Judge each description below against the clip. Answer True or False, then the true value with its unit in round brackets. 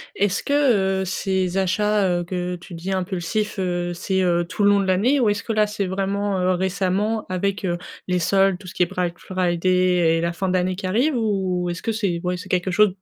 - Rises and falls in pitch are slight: True (2.1 semitones)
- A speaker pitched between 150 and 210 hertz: True (185 Hz)